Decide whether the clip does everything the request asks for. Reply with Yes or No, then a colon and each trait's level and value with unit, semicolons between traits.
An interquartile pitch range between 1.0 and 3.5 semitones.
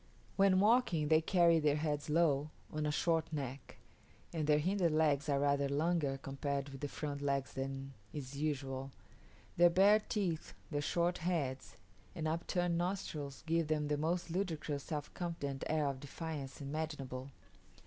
Yes: average, 3.2 semitones